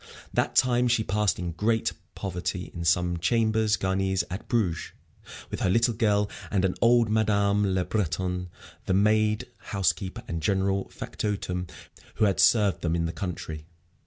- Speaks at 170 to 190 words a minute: No, average, 155 wpm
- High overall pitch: No, very low, 95 Hz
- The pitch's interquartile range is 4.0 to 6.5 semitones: No, average, 3.1 semitones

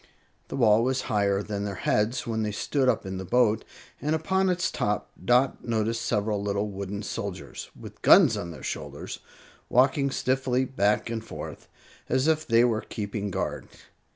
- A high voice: No, low, 115 Hz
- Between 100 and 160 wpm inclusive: No, average, 170 wpm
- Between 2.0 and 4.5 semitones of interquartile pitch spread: Yes, average, 4.0 semitones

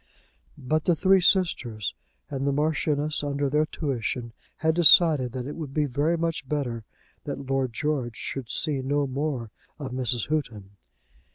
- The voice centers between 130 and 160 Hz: Yes, medium, 140 Hz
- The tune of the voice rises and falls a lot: No, average, 3.2 semitones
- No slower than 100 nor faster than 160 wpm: Yes, average, 155 wpm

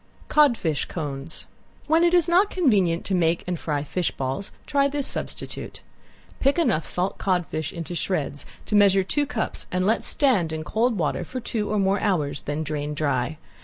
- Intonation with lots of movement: Yes, wide, 7.6 semitones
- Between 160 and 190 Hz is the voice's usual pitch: Yes, medium, 185 Hz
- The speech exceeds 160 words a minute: Yes, average, 175 wpm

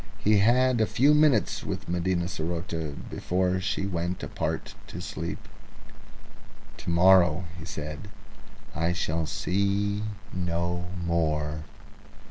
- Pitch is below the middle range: Yes, very low, 90 Hz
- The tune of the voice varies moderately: Yes, average, 3.1 semitones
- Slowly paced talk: Yes, slow, 110 wpm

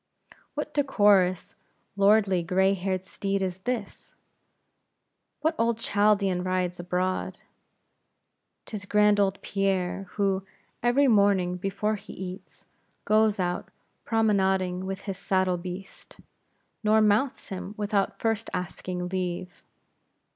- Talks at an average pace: No, slow, 110 wpm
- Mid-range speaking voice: No, high, 195 Hz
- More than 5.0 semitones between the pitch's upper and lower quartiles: No, narrow, 2.4 semitones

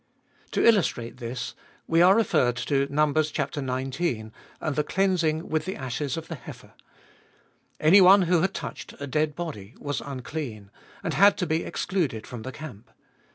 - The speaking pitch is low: No, medium, 150 Hz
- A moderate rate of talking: Yes, average, 155 wpm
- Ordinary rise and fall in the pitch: Yes, average, 4.9 semitones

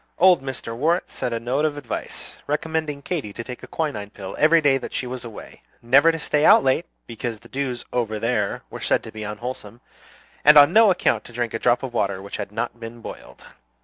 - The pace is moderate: No, fast, 220 wpm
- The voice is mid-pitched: No, low, 125 Hz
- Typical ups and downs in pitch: Yes, average, 4.5 semitones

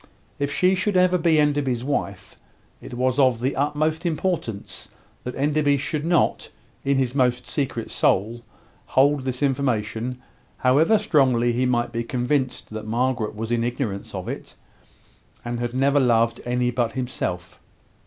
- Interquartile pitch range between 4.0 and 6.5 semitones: No, average, 3.4 semitones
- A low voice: Yes, low, 130 Hz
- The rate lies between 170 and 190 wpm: No, average, 150 wpm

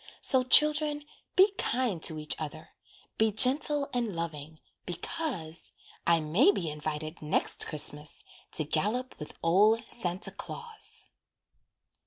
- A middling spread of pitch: No, wide, 8.7 semitones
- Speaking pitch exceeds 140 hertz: Yes, high, 190 Hz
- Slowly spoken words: Yes, slow, 120 wpm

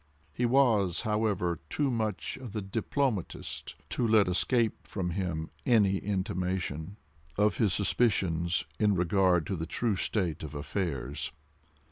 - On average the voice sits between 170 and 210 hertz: No, very low, 95 Hz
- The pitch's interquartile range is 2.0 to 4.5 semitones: Yes, average, 4.1 semitones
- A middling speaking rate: No, slow, 125 wpm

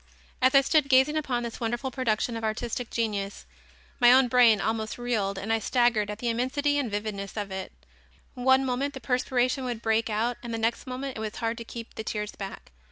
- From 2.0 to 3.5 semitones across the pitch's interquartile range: Yes, average, 2.8 semitones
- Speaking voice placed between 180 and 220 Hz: No, high, 235 Hz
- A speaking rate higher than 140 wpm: Yes, fast, 205 wpm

